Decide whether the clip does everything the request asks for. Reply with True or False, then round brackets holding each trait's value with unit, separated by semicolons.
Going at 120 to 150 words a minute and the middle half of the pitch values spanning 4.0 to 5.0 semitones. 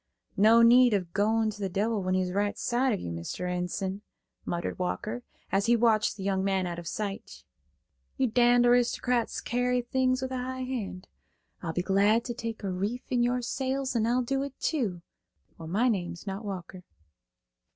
False (185 wpm; 4.4 semitones)